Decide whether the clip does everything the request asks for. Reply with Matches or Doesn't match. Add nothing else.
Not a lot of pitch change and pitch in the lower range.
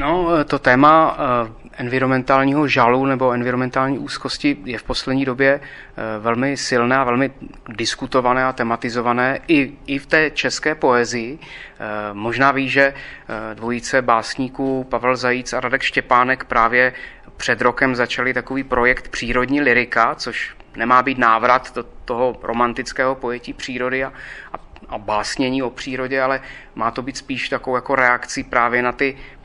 Matches